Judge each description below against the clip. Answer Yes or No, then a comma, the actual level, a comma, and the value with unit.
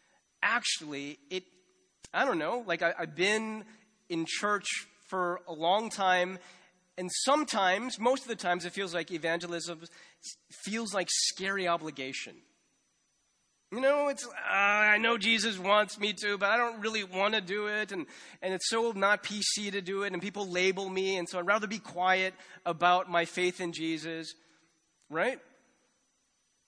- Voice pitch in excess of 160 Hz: Yes, high, 190 Hz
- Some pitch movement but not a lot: Yes, average, 3.6 semitones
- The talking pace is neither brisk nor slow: Yes, average, 160 wpm